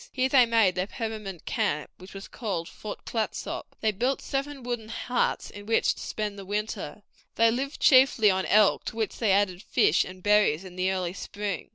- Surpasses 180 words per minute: Yes, average, 195 wpm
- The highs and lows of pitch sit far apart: No, average, 3.3 semitones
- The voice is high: Yes, high, 210 Hz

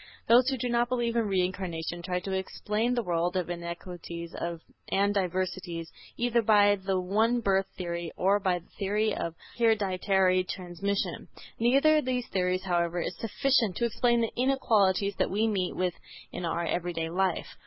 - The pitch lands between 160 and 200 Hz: Yes, high, 190 Hz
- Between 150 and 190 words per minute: Yes, average, 165 wpm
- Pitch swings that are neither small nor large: Yes, average, 4.2 semitones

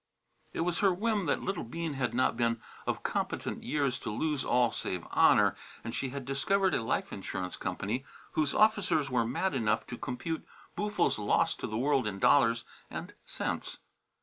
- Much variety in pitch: Yes, wide, 6.5 semitones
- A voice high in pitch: No, low, 135 Hz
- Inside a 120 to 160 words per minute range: No, average, 175 wpm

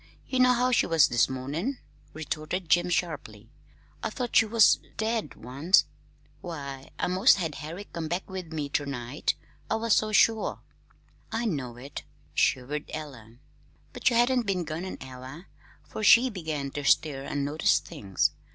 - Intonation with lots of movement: Yes, wide, 7.0 semitones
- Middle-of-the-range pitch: Yes, medium, 160 Hz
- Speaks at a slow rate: No, average, 165 wpm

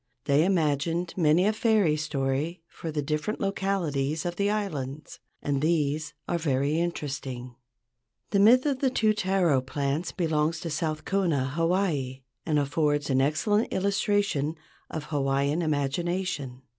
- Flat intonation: No, average, 4.6 semitones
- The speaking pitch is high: No, medium, 155 Hz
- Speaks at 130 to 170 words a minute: Yes, slow, 135 wpm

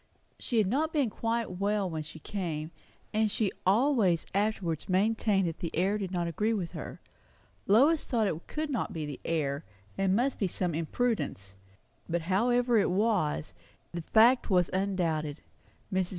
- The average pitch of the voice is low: No, high, 195 Hz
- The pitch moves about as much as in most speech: Yes, average, 5.0 semitones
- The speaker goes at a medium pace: Yes, average, 165 wpm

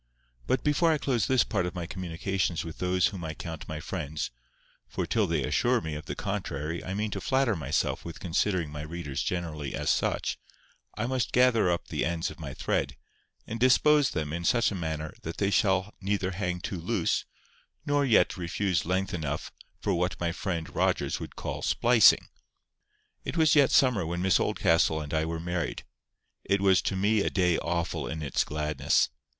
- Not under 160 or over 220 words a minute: Yes, average, 190 wpm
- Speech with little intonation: No, average, 4.2 semitones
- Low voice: Yes, very low, 90 Hz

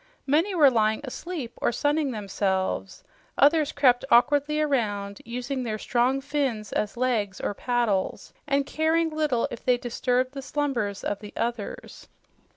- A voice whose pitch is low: No, very high, 250 Hz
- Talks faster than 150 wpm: No, average, 145 wpm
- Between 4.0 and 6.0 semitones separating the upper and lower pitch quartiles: Yes, average, 4.9 semitones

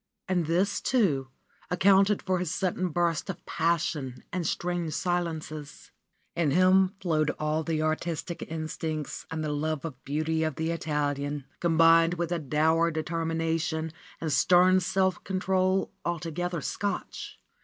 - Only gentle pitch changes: Yes, narrow, 2.3 semitones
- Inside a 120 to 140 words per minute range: Yes, slow, 135 wpm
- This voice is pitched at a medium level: Yes, medium, 165 Hz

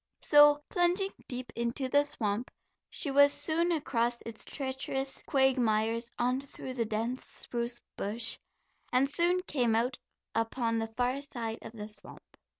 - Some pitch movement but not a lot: Yes, average, 3.6 semitones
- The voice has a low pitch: No, very high, 250 Hz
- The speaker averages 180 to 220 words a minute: No, average, 145 wpm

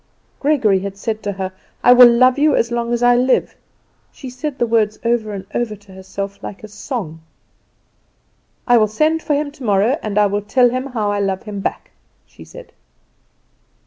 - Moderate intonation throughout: Yes, average, 3.8 semitones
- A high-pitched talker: Yes, high, 230 Hz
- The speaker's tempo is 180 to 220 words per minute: Yes, average, 190 wpm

